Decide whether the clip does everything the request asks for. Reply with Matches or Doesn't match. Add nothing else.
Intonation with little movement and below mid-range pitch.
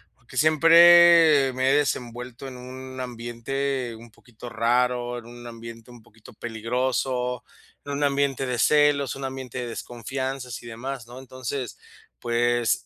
Matches